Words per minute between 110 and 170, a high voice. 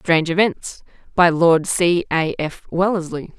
No: average, 140 wpm; medium, 170 Hz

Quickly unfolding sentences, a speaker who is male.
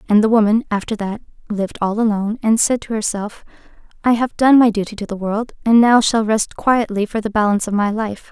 No: fast, 225 wpm; female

